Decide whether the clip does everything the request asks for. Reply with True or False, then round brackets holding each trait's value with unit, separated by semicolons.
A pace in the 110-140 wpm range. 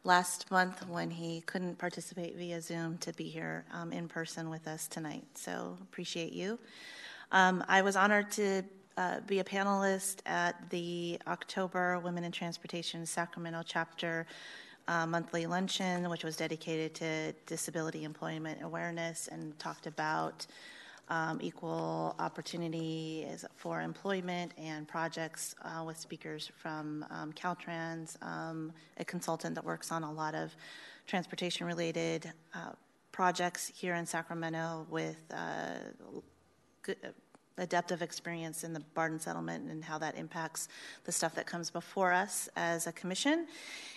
True (135 wpm)